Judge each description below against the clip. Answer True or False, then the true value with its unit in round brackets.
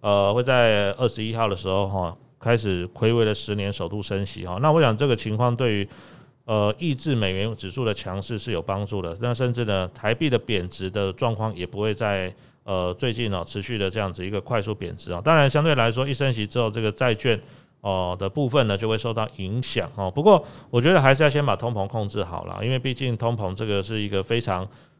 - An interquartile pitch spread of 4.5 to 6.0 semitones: False (3.8 semitones)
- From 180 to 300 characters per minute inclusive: False (330 characters per minute)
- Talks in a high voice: False (110 Hz)